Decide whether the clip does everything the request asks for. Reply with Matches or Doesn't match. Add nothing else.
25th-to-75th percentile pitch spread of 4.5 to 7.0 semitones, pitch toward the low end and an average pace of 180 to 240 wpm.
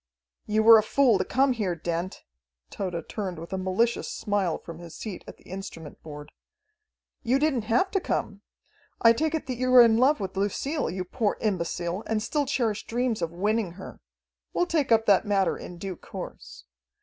Doesn't match